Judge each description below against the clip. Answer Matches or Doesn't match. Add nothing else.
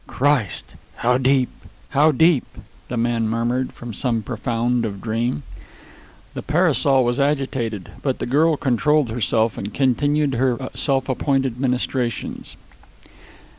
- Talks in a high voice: Doesn't match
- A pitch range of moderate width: Matches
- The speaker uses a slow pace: Matches